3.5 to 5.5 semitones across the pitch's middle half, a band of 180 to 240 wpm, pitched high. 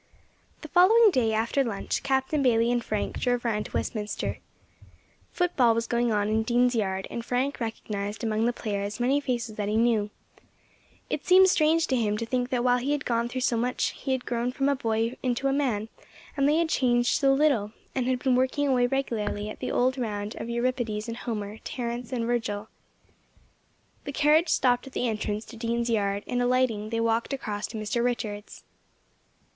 No: average, 2.9 semitones; average, 195 wpm; high, 240 Hz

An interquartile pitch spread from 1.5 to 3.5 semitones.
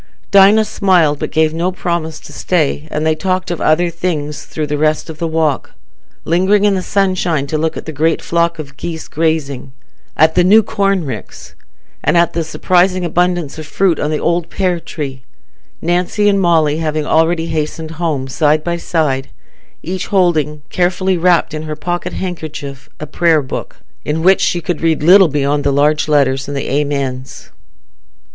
Yes: average, 2.8 semitones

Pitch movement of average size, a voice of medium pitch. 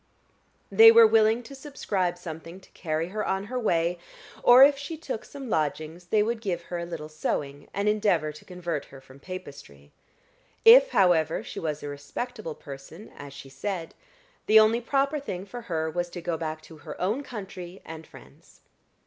No: wide, 5.9 semitones; medium, 180 Hz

